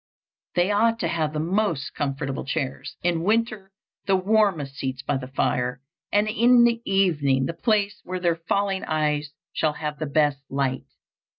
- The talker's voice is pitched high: No, medium, 165 Hz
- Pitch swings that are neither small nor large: No, wide, 6.3 semitones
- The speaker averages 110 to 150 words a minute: No, average, 165 wpm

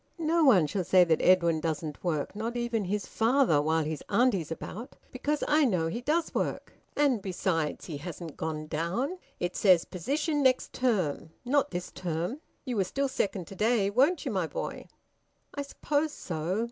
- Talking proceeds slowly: No, average, 175 wpm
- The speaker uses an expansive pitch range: Yes, wide, 8.0 semitones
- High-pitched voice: Yes, high, 200 Hz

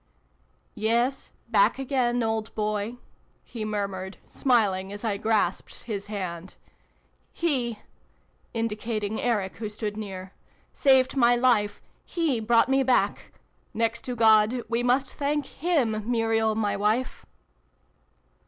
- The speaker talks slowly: Yes, slow, 130 wpm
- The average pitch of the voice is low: No, high, 225 Hz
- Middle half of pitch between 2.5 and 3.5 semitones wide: Yes, average, 2.8 semitones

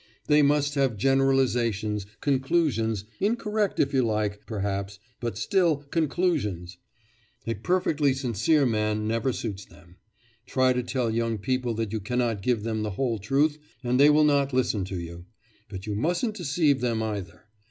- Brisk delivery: No, average, 155 wpm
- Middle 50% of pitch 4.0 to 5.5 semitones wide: Yes, average, 5.0 semitones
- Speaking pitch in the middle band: No, low, 120 Hz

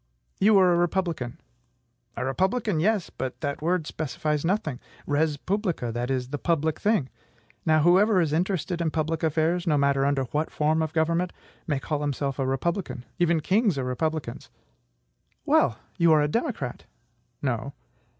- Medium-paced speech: Yes, average, 160 wpm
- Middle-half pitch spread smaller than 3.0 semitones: No, average, 4.0 semitones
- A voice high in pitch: No, medium, 155 Hz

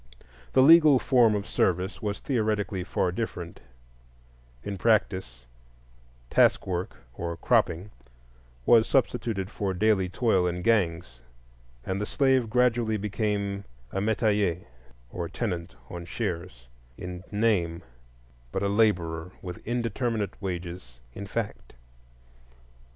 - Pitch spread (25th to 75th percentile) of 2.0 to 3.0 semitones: No, average, 4.0 semitones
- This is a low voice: Yes, low, 100 Hz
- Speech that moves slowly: Yes, slow, 110 wpm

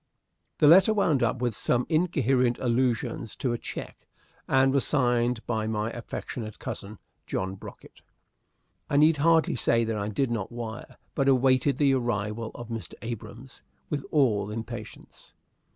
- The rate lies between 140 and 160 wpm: Yes, average, 150 wpm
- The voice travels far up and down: No, average, 3.3 semitones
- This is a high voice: No, low, 120 Hz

